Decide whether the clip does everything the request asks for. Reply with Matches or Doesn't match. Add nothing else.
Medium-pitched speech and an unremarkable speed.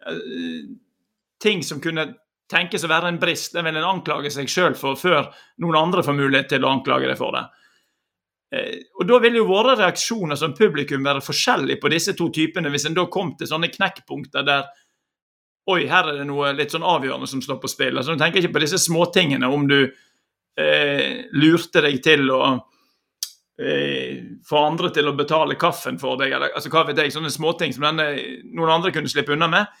Matches